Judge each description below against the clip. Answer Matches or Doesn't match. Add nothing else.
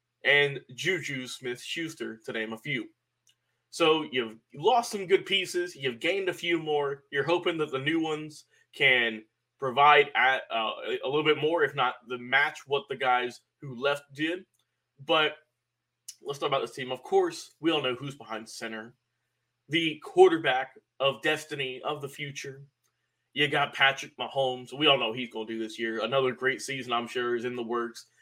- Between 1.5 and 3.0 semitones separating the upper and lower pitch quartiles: Doesn't match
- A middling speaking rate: Matches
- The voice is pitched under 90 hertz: Doesn't match